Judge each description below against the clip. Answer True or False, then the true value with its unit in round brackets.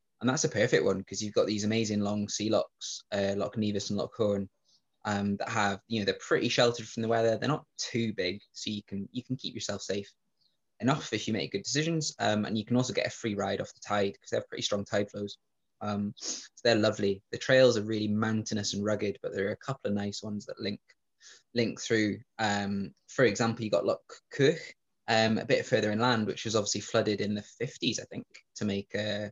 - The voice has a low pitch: True (105 Hz)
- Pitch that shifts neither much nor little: False (1.9 semitones)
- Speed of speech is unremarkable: False (235 wpm)